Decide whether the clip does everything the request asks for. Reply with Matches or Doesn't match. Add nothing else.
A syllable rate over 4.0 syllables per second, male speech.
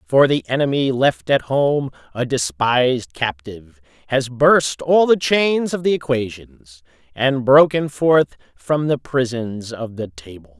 Doesn't match